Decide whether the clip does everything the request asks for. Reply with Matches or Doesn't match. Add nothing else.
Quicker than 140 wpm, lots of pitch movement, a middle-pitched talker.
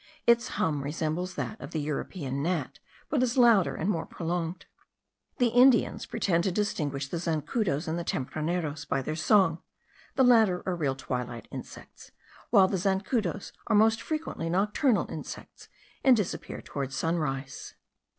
Matches